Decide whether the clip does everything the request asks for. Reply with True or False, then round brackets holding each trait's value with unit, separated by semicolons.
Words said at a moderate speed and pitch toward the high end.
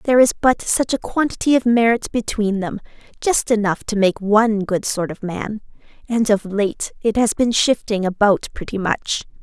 True (185 wpm; 215 Hz)